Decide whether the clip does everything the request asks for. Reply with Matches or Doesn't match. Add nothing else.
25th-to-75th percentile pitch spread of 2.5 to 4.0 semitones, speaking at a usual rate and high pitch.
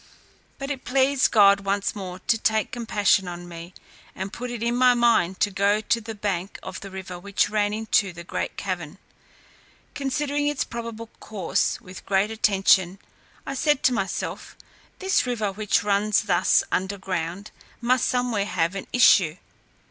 Matches